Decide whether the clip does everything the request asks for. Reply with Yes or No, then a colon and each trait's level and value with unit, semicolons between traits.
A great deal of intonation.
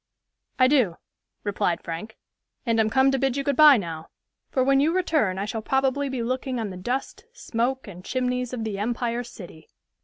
No: average, 4.2 semitones